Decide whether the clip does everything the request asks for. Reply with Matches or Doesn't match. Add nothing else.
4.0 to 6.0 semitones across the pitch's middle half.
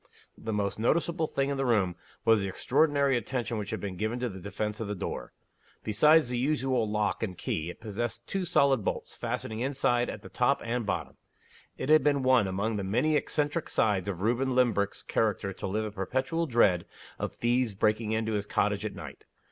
Matches